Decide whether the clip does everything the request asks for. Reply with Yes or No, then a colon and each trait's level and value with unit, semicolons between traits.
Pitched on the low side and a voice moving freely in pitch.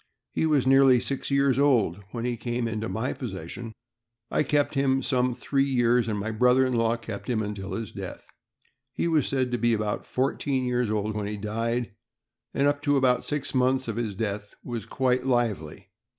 No: low, 120 Hz; average, 3.2 semitones